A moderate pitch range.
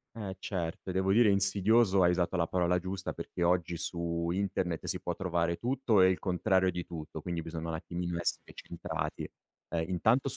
No: narrow, 2.2 semitones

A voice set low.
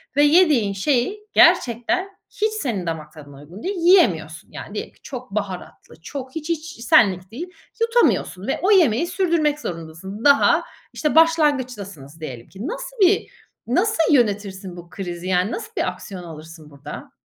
No: high, 235 Hz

